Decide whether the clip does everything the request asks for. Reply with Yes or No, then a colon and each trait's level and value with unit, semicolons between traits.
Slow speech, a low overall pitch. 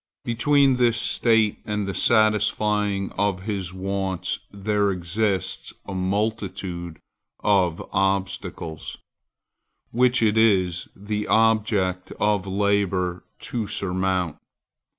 Yes: slow, 95 wpm; low, 100 Hz